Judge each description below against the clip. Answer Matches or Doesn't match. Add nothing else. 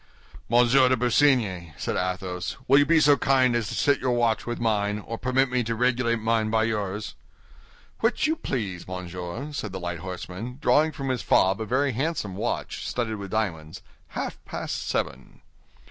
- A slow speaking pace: Doesn't match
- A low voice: Matches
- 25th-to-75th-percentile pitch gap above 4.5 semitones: Matches